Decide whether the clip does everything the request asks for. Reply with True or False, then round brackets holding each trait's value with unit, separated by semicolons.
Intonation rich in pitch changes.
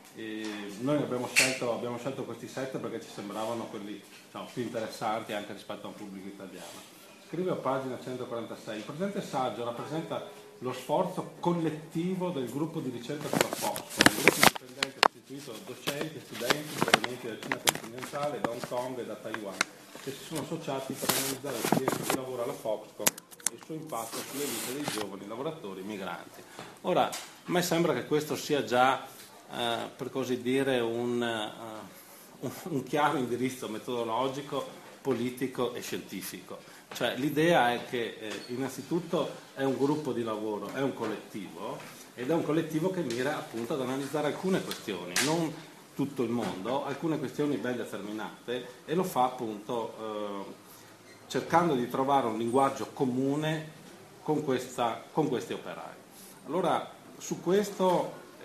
False (4.3 semitones)